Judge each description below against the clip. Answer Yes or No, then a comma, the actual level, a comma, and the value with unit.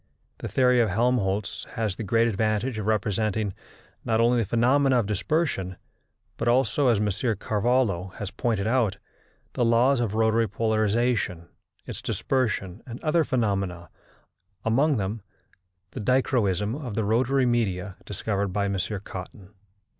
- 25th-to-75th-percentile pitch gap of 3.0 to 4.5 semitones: Yes, average, 3.5 semitones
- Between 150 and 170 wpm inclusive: No, average, 140 wpm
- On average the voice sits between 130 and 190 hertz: No, low, 110 Hz